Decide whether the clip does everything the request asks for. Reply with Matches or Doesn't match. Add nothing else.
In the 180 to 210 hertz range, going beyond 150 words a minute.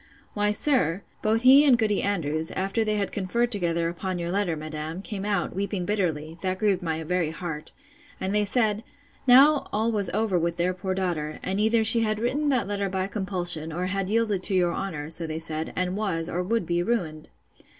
Matches